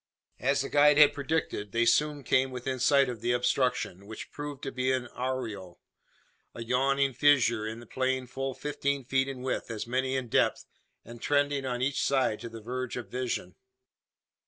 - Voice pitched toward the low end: Yes, low, 130 Hz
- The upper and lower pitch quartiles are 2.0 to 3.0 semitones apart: Yes, narrow, 2.5 semitones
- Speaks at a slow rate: No, average, 180 wpm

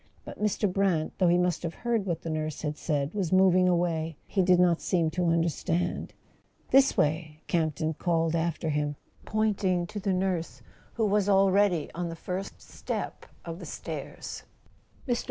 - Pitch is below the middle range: No, medium, 175 Hz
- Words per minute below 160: No, average, 175 wpm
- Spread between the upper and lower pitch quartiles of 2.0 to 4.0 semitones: Yes, average, 2.9 semitones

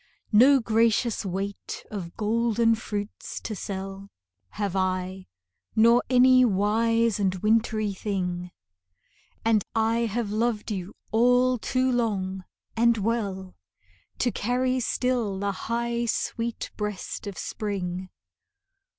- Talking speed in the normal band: No, slow, 110 wpm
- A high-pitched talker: Yes, high, 215 Hz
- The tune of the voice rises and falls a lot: No, average, 3.2 semitones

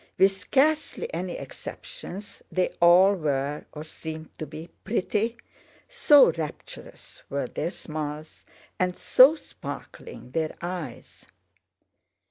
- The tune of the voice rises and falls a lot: Yes, wide, 6.7 semitones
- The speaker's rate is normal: No, slow, 100 wpm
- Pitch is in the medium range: Yes, medium, 175 Hz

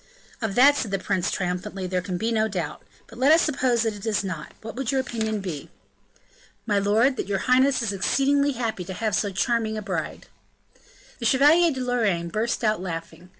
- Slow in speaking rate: No, average, 200 wpm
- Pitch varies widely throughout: No, average, 4.9 semitones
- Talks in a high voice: Yes, high, 220 Hz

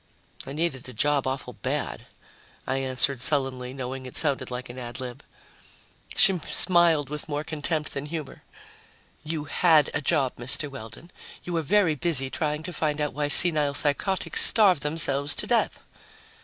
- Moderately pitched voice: Yes, medium, 145 Hz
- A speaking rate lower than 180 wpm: Yes, average, 160 wpm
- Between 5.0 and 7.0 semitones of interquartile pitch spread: No, average, 3.2 semitones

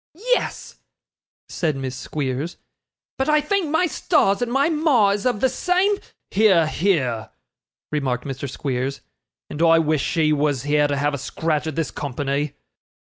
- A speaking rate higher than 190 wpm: No, average, 160 wpm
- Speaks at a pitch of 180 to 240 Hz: No, medium, 155 Hz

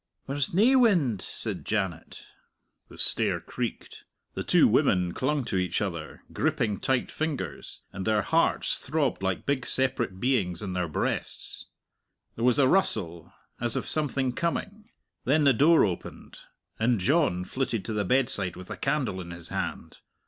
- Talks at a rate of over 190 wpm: No, average, 155 wpm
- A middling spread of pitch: No, wide, 7.3 semitones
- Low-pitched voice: Yes, low, 120 Hz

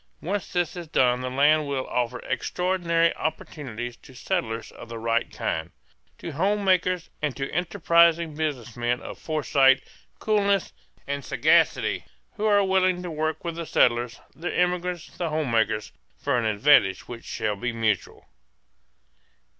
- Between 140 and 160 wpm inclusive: Yes, average, 150 wpm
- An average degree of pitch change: No, wide, 6.3 semitones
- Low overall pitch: No, medium, 150 Hz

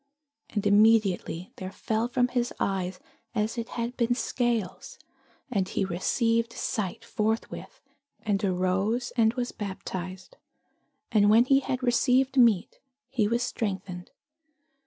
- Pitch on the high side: Yes, high, 220 Hz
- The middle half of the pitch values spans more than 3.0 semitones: Yes, average, 3.8 semitones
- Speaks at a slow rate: Yes, slow, 125 wpm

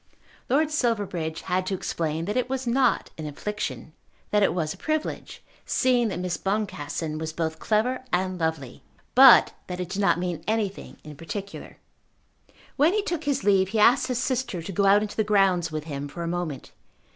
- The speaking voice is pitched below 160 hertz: No, high, 195 Hz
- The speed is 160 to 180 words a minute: No, average, 190 wpm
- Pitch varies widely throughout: Yes, wide, 6.5 semitones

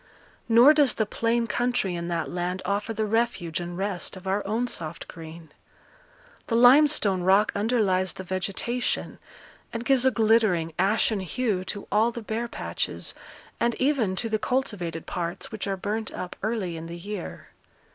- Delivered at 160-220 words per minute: Yes, average, 165 wpm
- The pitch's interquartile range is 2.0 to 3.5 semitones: No, average, 4.3 semitones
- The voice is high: Yes, high, 210 Hz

